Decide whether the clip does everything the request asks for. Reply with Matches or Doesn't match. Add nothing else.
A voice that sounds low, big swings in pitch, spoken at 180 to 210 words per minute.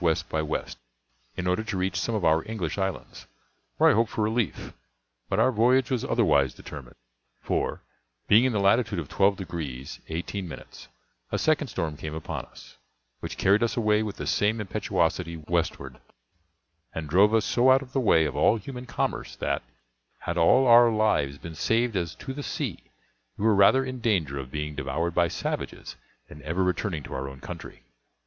Matches